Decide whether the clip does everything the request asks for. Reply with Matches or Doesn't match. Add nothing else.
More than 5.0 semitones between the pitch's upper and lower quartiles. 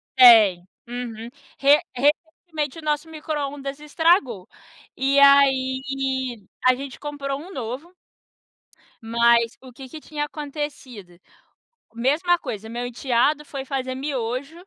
Doesn't match